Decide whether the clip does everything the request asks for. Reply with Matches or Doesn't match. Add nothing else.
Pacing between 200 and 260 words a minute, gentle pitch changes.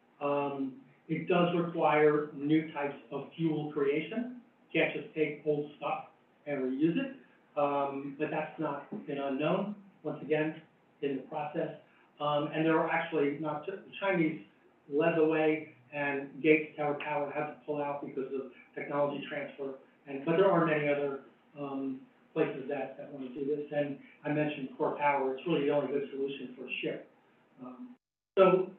Doesn't match